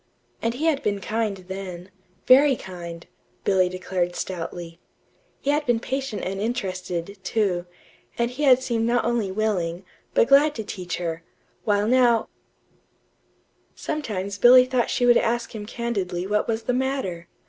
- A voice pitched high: Yes, high, 215 Hz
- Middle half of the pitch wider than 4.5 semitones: Yes, average, 4.9 semitones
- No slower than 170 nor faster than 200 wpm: No, average, 150 wpm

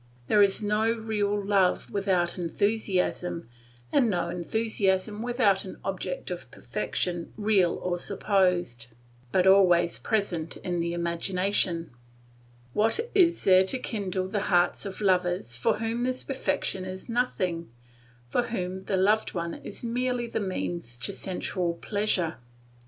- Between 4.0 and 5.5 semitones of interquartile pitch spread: No, average, 3.4 semitones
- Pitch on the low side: No, high, 190 Hz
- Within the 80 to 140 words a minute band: Yes, slow, 135 wpm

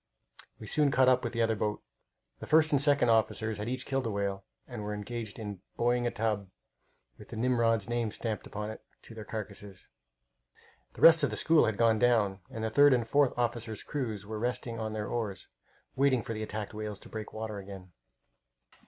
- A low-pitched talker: Yes, low, 110 Hz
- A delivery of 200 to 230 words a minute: Yes, fast, 205 wpm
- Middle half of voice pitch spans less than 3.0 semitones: Yes, narrow, 2.5 semitones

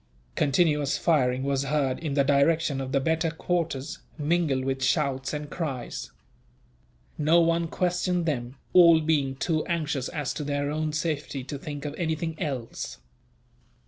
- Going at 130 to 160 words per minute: Yes, average, 145 wpm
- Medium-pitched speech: Yes, medium, 150 Hz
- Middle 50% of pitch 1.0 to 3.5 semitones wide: Yes, average, 3.1 semitones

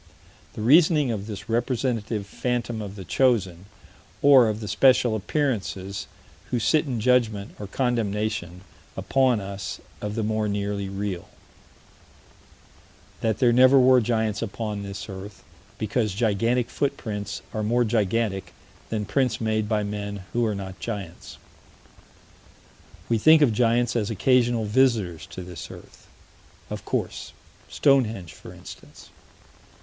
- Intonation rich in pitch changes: No, average, 3.3 semitones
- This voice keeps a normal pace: No, slow, 130 wpm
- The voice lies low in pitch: Yes, low, 110 Hz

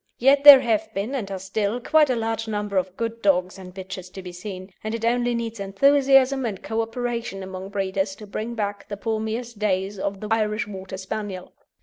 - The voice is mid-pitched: No, high, 210 Hz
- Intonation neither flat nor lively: Yes, average, 3.4 semitones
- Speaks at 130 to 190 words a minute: No, fast, 205 wpm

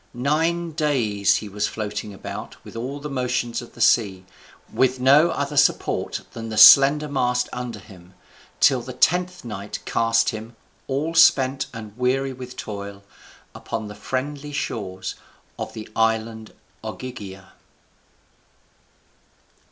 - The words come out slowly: Yes, slow, 130 wpm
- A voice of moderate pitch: No, low, 125 Hz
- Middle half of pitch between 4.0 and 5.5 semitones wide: Yes, average, 4.3 semitones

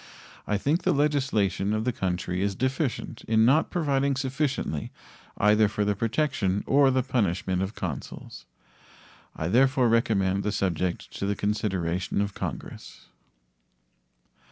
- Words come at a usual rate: No, slow, 130 wpm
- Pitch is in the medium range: No, low, 105 Hz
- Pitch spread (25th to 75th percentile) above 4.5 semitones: Yes, wide, 5.4 semitones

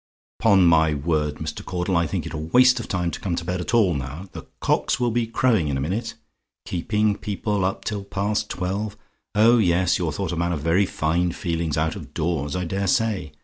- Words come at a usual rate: No, fast, 220 wpm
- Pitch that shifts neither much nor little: Yes, average, 4.3 semitones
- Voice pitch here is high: No, very low, 90 Hz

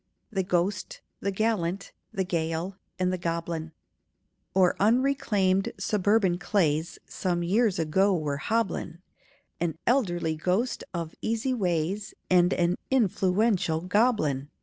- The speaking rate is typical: No, slow, 115 wpm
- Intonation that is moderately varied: Yes, average, 3.6 semitones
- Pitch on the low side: No, medium, 185 Hz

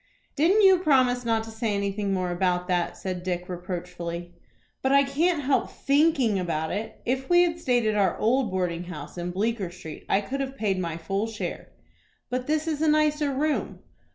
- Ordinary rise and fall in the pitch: No, wide, 7.5 semitones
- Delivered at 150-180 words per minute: No, average, 190 wpm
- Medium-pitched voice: No, high, 220 Hz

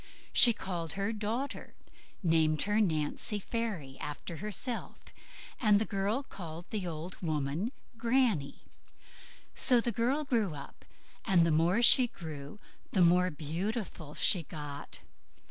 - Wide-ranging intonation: Yes, wide, 5.9 semitones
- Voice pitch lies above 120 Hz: Yes, medium, 185 Hz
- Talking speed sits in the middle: No, slow, 130 wpm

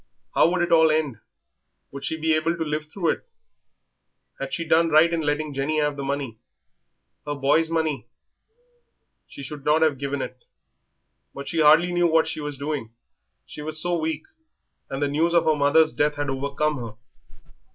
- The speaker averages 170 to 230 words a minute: Yes, average, 185 wpm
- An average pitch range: No, narrow, 2.2 semitones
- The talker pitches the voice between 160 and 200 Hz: No, medium, 150 Hz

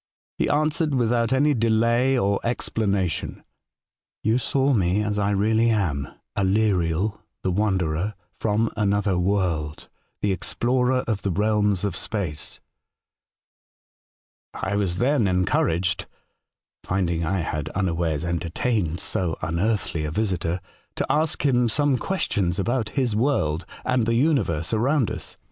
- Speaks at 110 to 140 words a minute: Yes, slow, 135 wpm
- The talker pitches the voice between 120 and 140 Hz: No, low, 105 Hz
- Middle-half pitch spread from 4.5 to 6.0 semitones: Yes, average, 4.9 semitones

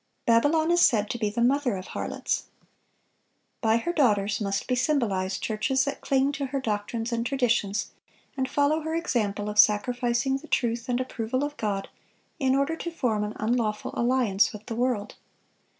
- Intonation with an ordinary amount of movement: Yes, average, 4.2 semitones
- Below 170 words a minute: No, average, 175 wpm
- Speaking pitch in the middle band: No, high, 240 Hz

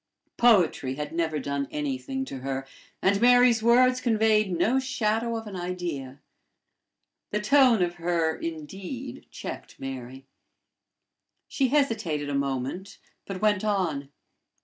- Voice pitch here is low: No, high, 190 Hz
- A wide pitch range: Yes, wide, 8.0 semitones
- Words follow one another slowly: Yes, slow, 125 wpm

